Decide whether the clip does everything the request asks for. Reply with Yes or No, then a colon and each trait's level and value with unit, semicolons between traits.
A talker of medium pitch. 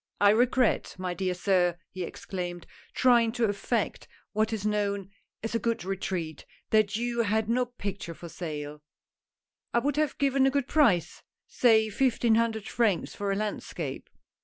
No: high, 215 Hz